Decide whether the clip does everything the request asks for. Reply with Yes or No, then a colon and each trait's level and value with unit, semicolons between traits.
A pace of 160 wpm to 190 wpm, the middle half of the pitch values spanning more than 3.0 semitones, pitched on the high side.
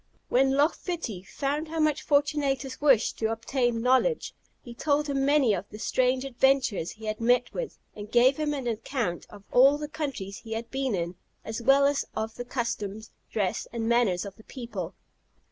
Yes: average, 185 wpm; average, 4.1 semitones; high, 245 Hz